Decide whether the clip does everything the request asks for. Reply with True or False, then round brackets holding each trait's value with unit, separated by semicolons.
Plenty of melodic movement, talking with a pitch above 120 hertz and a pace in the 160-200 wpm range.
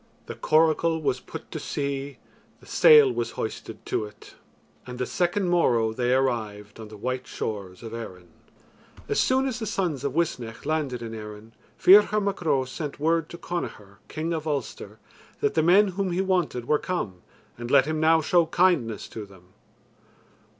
True (7.0 semitones; 140 Hz; 175 wpm)